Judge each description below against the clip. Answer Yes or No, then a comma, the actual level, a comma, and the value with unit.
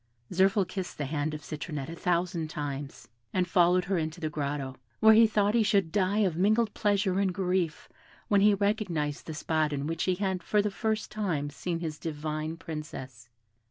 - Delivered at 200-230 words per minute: No, average, 190 wpm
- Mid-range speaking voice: Yes, medium, 175 Hz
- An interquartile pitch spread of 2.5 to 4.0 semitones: No, average, 4.6 semitones